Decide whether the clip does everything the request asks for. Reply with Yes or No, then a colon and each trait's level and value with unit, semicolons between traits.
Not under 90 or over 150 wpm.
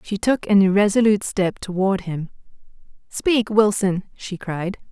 Yes: slow, 135 wpm